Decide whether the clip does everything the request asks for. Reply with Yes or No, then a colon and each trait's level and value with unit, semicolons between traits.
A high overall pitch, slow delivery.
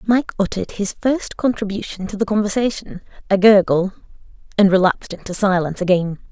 Yes: high, 200 Hz; slow, 125 wpm